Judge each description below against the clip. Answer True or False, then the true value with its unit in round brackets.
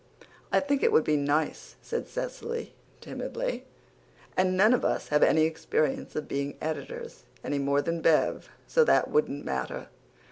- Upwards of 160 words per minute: False (155 wpm)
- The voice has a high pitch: False (165 Hz)